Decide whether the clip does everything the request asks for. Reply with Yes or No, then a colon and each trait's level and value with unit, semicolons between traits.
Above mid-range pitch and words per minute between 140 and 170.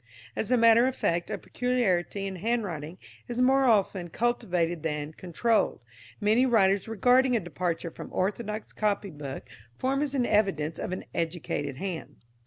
Yes: high, 200 Hz; average, 150 wpm